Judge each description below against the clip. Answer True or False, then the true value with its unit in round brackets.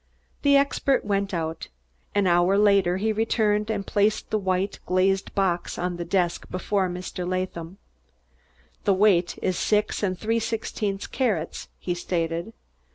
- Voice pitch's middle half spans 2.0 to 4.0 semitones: True (2.9 semitones)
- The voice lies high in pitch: True (195 Hz)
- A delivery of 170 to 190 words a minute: False (145 wpm)